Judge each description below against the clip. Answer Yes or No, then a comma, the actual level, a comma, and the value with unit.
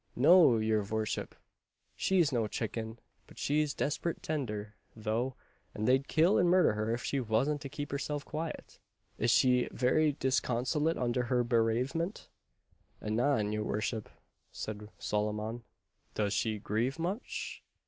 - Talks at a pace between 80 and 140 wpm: Yes, slow, 135 wpm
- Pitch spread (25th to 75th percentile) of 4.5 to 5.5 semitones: Yes, average, 5.1 semitones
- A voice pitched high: No, low, 125 Hz